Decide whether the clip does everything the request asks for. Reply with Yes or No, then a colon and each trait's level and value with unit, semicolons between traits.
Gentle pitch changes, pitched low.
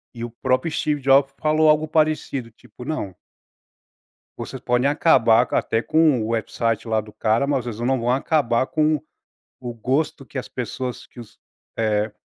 No: average, 4.2 semitones; low, 130 Hz